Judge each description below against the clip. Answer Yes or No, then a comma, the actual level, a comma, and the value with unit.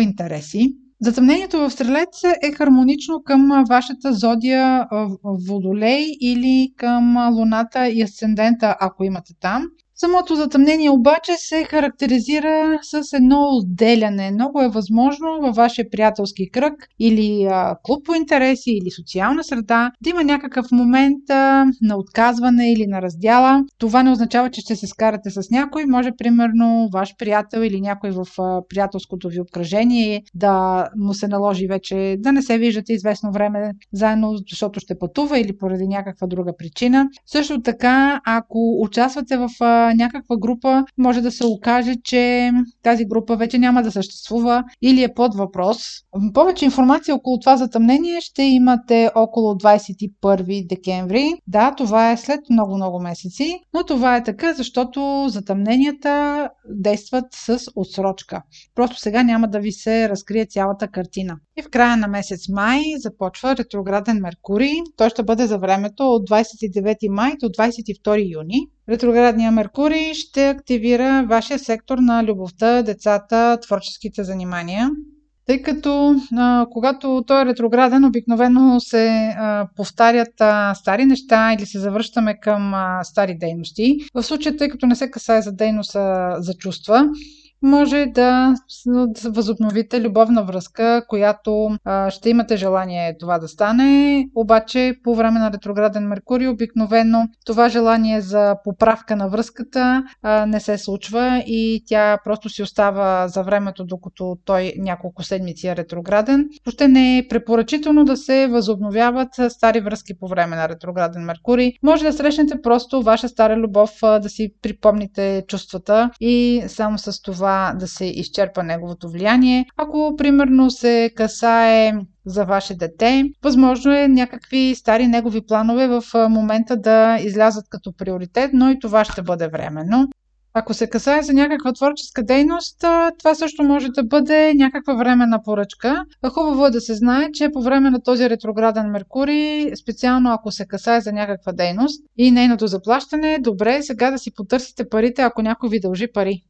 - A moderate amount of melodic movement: Yes, average, 4.1 semitones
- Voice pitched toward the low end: No, high, 230 Hz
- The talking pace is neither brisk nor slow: Yes, average, 145 wpm